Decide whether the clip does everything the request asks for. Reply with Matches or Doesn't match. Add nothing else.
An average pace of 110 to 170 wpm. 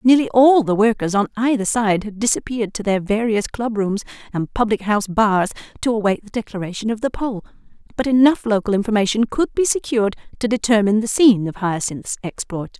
Doesn't match